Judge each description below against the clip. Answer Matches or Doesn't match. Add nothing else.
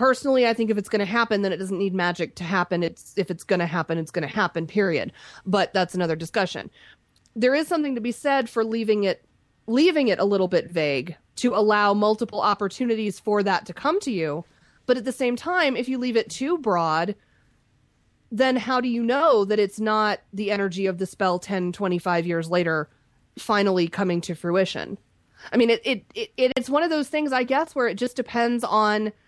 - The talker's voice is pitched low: Doesn't match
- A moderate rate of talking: Doesn't match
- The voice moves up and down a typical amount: Doesn't match